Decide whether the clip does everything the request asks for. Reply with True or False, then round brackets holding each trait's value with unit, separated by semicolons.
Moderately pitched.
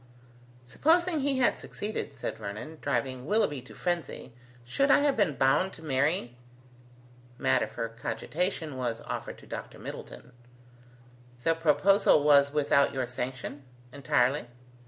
True (145 Hz)